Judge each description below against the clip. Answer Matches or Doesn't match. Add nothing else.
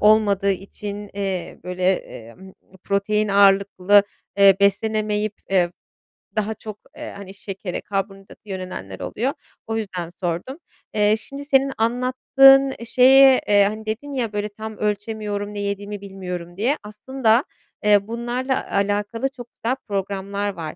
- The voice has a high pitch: Matches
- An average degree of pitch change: Doesn't match